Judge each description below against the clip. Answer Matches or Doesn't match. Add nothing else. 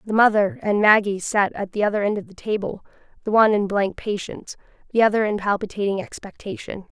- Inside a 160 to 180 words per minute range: Doesn't match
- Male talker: Doesn't match